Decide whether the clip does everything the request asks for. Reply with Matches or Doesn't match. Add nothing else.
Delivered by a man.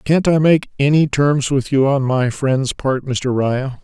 Matches